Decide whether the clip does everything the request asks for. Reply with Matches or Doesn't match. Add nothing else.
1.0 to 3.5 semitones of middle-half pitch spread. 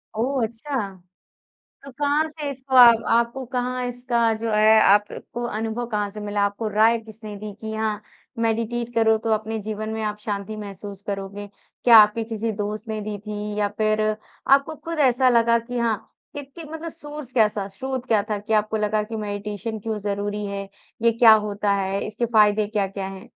Matches